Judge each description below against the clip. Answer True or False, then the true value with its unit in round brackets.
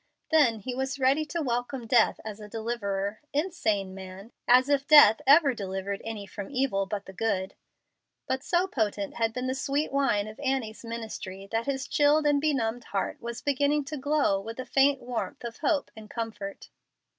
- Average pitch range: True (5.0 semitones)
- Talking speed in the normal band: True (180 wpm)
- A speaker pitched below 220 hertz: False (240 Hz)